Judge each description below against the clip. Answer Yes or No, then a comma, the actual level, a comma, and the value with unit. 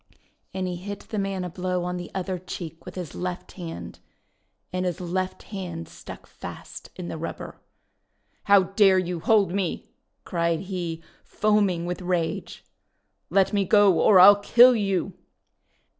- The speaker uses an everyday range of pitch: No, narrow, 2.0 semitones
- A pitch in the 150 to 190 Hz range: Yes, medium, 185 Hz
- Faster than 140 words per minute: Yes, average, 160 wpm